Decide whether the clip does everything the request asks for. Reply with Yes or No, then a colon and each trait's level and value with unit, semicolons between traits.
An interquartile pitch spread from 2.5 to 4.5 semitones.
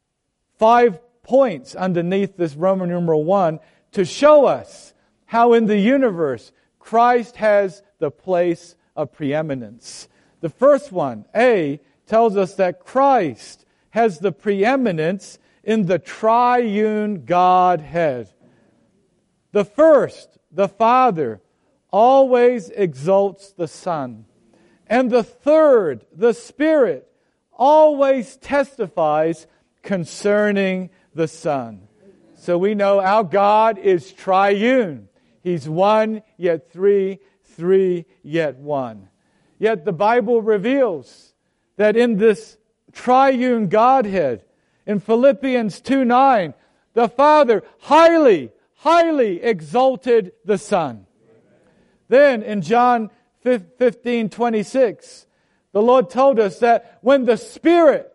No: wide, 5.5 semitones